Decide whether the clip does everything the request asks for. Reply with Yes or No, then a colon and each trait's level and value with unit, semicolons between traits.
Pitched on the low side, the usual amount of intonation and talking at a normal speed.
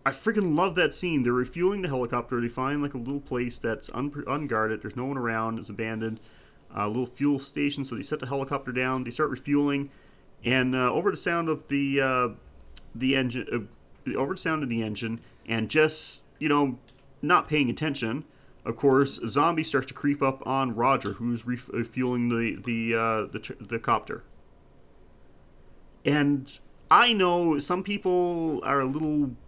Yes: low, 130 Hz; average, 3.7 semitones; average, 180 wpm